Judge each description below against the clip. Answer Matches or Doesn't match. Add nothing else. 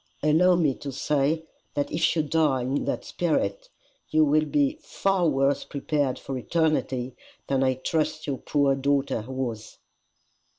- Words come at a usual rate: Matches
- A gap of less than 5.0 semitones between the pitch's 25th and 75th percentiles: Matches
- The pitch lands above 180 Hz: Doesn't match